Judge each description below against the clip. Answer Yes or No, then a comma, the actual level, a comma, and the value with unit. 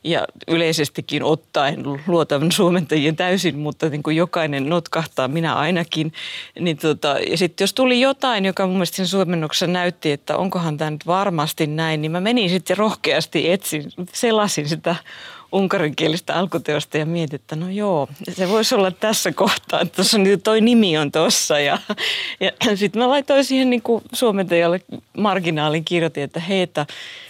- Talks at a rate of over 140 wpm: Yes, fast, 155 wpm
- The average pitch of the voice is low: No, medium, 175 Hz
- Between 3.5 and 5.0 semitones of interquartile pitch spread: Yes, average, 3.9 semitones